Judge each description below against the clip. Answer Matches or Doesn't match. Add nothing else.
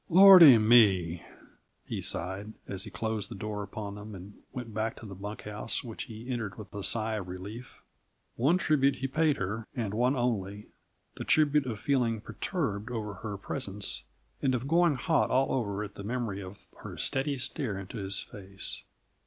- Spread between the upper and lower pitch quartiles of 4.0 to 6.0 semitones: Matches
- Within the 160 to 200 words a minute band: Matches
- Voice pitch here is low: Matches